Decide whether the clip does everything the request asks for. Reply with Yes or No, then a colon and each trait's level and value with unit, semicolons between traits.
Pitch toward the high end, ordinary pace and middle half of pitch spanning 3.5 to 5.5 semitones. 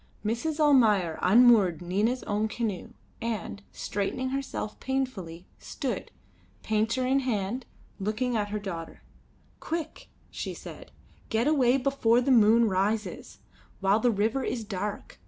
No: high, 225 Hz; slow, 125 wpm; average, 3.9 semitones